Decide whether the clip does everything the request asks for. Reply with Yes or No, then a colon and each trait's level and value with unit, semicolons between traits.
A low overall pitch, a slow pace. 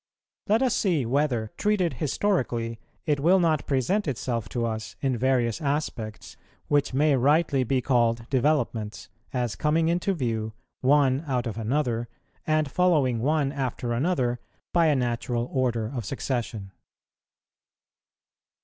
Yes: low, 130 Hz; slow, 130 wpm